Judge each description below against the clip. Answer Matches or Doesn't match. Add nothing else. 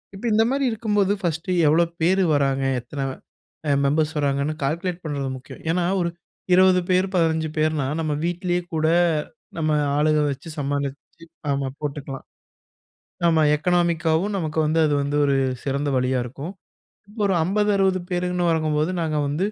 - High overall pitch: Doesn't match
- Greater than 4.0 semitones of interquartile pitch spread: Doesn't match